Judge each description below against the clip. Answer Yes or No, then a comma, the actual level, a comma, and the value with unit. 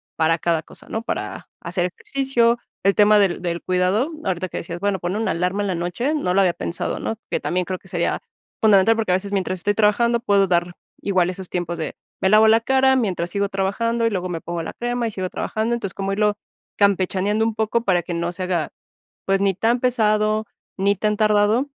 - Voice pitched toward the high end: Yes, high, 200 Hz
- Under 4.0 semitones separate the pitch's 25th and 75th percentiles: Yes, average, 3.4 semitones